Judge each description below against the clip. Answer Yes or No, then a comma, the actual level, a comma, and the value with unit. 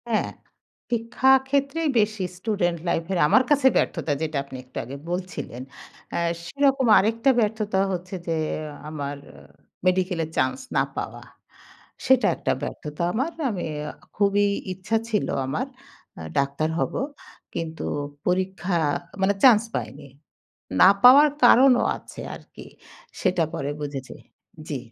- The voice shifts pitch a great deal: Yes, wide, 6.7 semitones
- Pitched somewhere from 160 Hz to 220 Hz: Yes, high, 190 Hz